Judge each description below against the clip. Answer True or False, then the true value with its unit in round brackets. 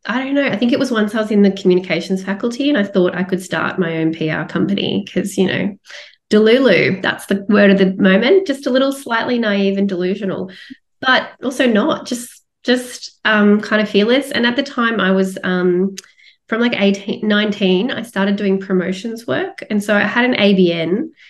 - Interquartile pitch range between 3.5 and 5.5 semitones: True (4.3 semitones)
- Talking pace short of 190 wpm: False (205 wpm)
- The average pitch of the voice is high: True (205 Hz)